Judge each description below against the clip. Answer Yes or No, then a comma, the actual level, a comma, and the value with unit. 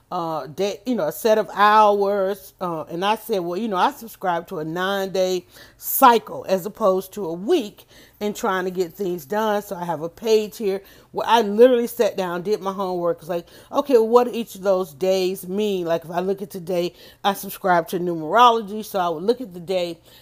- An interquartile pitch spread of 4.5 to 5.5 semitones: No, average, 3.2 semitones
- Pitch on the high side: Yes, high, 195 Hz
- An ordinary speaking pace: No, fast, 220 wpm